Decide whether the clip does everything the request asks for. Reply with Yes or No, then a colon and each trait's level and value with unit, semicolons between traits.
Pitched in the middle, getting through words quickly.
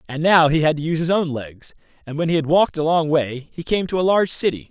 Yes: medium, 160 Hz; fast, 295 wpm